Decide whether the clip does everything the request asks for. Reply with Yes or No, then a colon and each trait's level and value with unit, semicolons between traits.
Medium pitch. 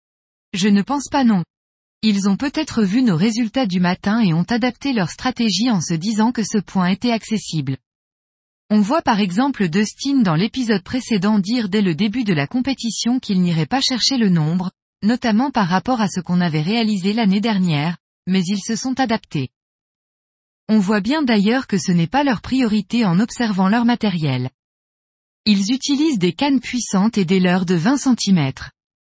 No: high, 215 Hz